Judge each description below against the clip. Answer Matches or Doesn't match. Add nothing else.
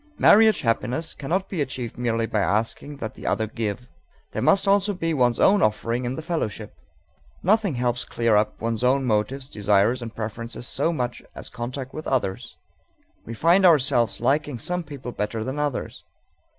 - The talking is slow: Doesn't match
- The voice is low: Matches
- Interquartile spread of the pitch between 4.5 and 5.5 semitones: Matches